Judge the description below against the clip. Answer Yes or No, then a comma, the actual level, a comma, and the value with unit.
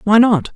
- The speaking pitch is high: Yes, high, 205 Hz